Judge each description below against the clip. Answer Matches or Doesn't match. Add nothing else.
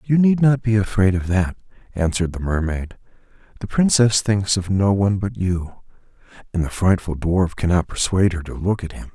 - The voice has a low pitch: Matches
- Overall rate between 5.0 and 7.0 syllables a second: Matches